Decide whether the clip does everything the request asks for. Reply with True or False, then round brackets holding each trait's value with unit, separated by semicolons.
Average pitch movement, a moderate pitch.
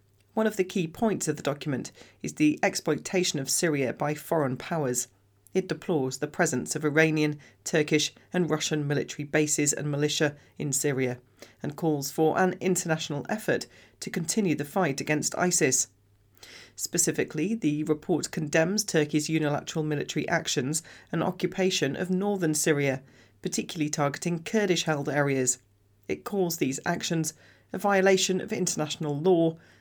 True (3.5 semitones; 155 Hz)